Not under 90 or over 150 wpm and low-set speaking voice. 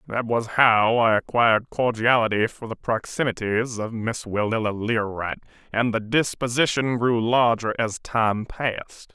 Yes: average, 140 wpm; low, 115 Hz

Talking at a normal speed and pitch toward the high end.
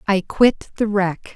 Yes: average, 175 wpm; high, 200 Hz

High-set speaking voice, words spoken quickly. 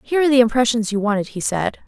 Yes: high, 230 Hz; fast, 255 wpm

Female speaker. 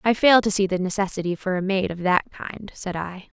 Yes: female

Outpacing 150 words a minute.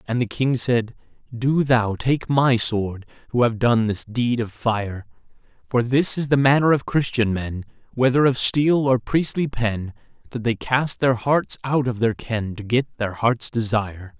Yes: average, 185 wpm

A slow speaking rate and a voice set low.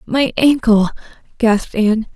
No: slow, 110 wpm; high, 230 Hz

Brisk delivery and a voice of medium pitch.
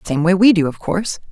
Yes: fast, 275 wpm; medium, 175 Hz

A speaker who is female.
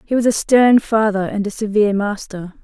Yes: female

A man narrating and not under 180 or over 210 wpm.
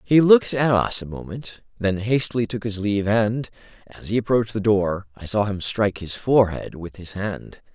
Yes: male; average, 200 wpm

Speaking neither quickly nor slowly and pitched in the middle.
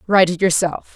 Yes: average, 190 wpm; medium, 180 Hz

